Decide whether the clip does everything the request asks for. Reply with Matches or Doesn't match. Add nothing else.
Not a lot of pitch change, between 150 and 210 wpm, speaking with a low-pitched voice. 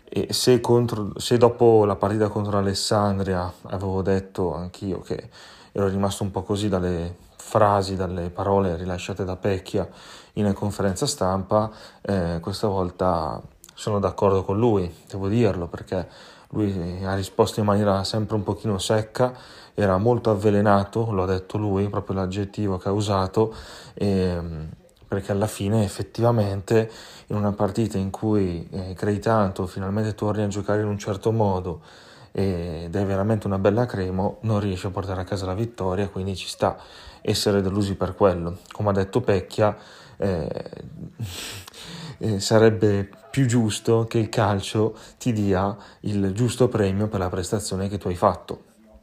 Matches